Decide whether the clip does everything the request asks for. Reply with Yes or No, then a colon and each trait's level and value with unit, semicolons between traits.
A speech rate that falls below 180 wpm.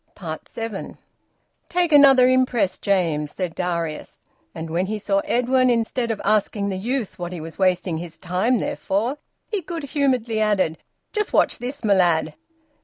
Yes: average, 160 wpm